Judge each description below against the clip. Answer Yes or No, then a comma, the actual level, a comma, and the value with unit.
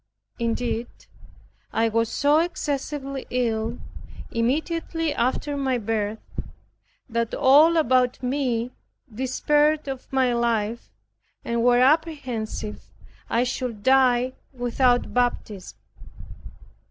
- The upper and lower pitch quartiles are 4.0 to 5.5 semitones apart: No, average, 3.1 semitones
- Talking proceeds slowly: Yes, slow, 90 wpm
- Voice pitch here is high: Yes, very high, 250 Hz